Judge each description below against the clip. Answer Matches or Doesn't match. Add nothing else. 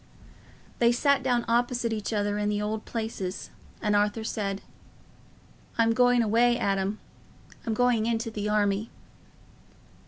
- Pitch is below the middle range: Doesn't match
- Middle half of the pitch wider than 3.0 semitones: Doesn't match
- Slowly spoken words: Matches